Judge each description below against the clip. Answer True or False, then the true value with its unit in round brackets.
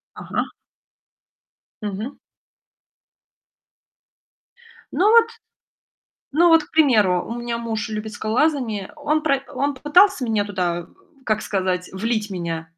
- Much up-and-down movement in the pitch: True (6.3 semitones)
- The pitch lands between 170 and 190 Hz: False (225 Hz)